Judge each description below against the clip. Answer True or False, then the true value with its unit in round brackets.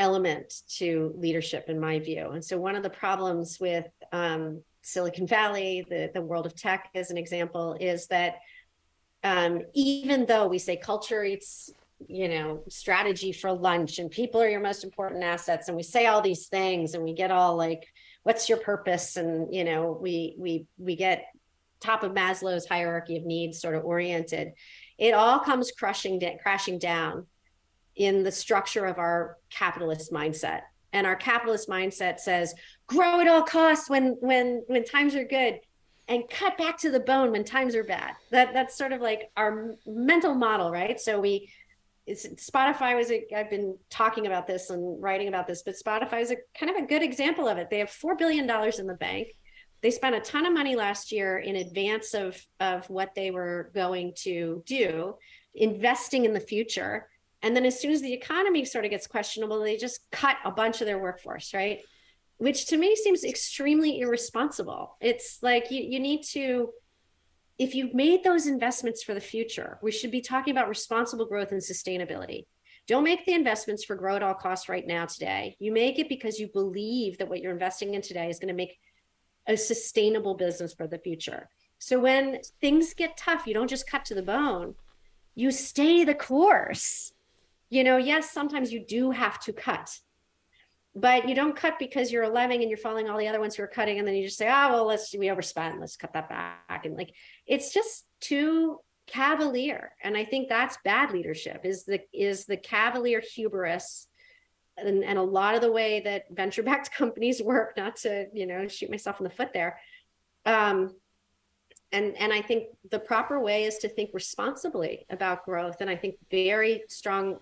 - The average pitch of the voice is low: False (210 Hz)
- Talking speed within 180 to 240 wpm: True (190 wpm)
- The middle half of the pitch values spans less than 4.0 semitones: False (5.4 semitones)